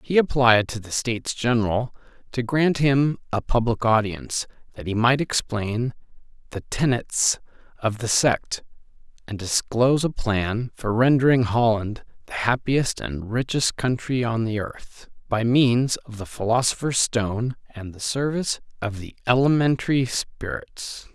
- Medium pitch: No, low, 120 Hz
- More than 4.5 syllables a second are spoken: No, 4.4 syllables/s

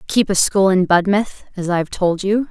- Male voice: No, female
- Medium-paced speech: No, fast, 240 wpm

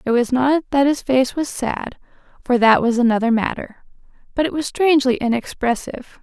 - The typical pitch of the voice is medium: No, very high, 260 Hz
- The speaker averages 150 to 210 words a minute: Yes, average, 175 wpm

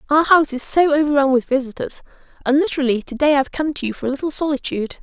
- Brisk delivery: Yes, fast, 240 wpm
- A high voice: Yes, very high, 280 Hz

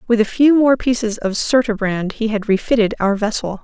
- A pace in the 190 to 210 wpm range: Yes, average, 200 wpm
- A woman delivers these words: Yes, female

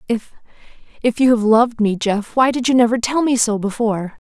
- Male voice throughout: No, female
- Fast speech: No, average, 195 wpm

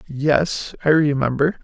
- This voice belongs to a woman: No, male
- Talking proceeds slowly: Yes, slow, 110 wpm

